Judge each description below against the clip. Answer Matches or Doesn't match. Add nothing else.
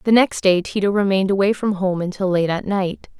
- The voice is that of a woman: Matches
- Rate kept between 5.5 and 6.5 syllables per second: Matches